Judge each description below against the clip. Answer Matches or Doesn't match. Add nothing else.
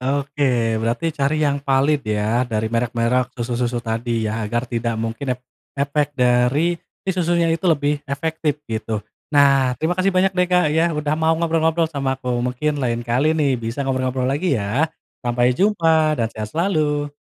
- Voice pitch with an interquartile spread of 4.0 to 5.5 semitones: Matches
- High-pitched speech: Doesn't match